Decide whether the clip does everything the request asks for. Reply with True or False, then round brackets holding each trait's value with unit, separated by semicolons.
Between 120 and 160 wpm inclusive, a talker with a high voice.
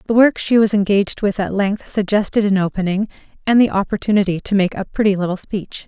False (205 wpm; 200 Hz)